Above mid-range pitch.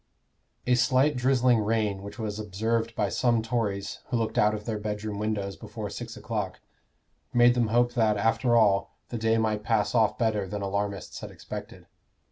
No: low, 110 Hz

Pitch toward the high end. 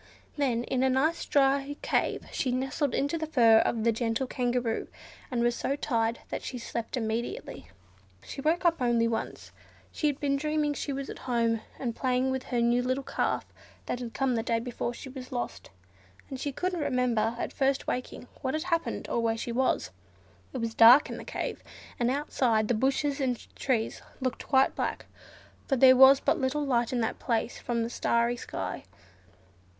Yes: very high, 255 Hz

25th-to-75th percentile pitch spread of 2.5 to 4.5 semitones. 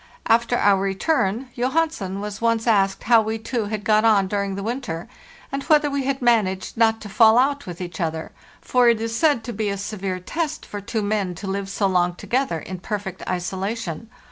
Yes: average, 3.6 semitones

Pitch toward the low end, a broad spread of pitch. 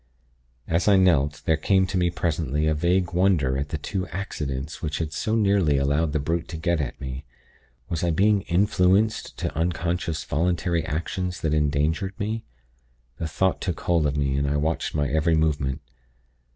No: very low, 80 Hz; average, 3.5 semitones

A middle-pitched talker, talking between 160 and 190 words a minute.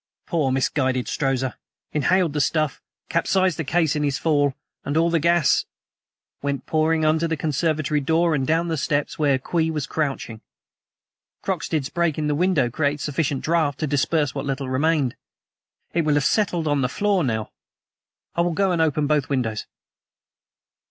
Yes: medium, 150 Hz; average, 165 wpm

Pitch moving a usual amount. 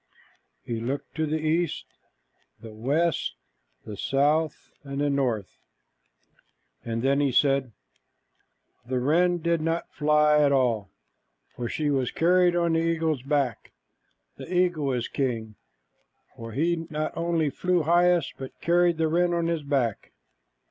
Yes: average, 4.2 semitones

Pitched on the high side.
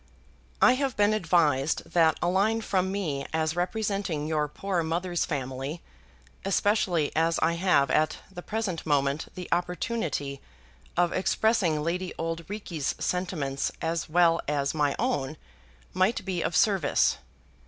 No: medium, 170 Hz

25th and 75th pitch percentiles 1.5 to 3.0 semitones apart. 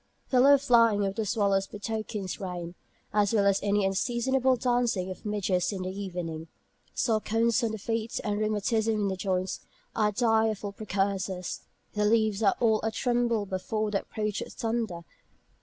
Yes: average, 2.7 semitones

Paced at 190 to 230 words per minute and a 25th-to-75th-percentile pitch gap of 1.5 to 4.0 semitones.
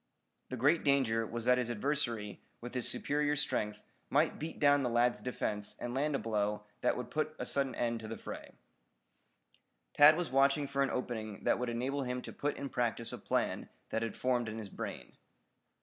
Yes: average, 195 wpm; average, 3.6 semitones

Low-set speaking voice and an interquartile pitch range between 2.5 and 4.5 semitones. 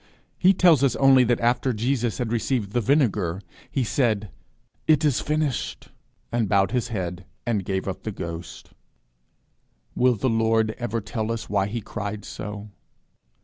Yes: low, 115 Hz; average, 3.7 semitones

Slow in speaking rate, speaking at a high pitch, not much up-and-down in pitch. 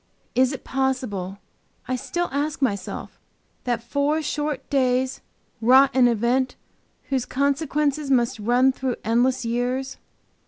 Yes: slow, 120 wpm; very high, 260 Hz; narrow, 2.2 semitones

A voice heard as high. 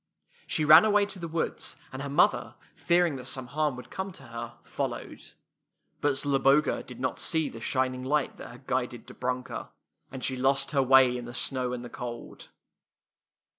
No: low, 135 Hz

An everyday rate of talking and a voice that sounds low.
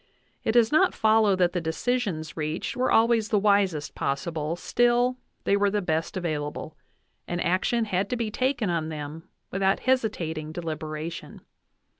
No: average, 155 wpm; medium, 185 Hz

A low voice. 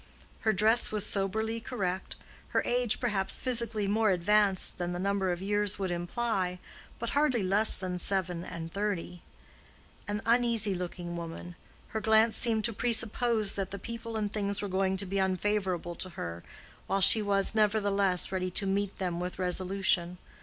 No: high, 200 Hz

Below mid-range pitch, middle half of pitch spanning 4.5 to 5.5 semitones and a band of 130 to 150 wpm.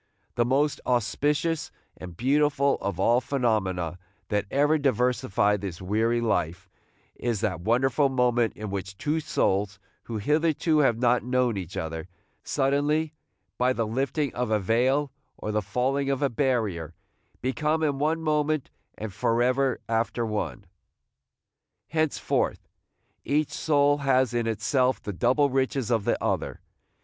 Yes: low, 125 Hz; average, 5.0 semitones; average, 140 wpm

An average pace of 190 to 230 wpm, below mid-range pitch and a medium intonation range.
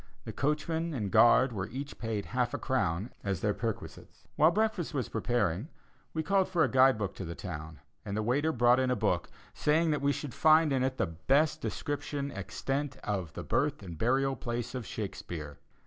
No: average, 195 wpm; low, 130 Hz; wide, 6.2 semitones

